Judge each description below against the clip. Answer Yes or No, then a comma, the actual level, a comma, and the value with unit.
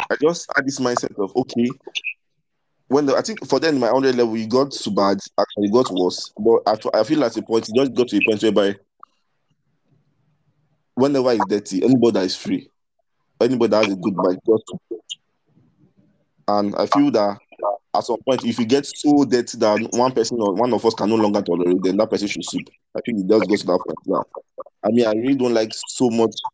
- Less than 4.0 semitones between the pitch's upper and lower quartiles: No, average, 4.5 semitones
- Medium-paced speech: No, fast, 235 wpm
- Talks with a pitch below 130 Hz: Yes, low, 115 Hz